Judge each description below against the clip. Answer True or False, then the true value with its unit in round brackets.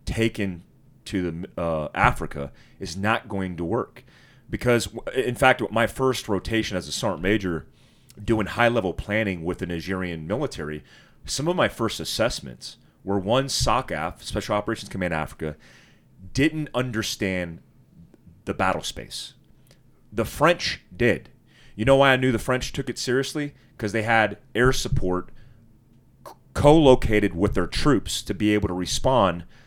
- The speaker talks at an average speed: True (150 wpm)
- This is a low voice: True (105 Hz)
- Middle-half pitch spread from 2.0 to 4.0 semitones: False (5.2 semitones)